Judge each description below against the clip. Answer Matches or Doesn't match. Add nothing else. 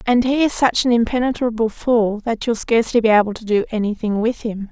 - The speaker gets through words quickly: Matches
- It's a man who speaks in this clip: Doesn't match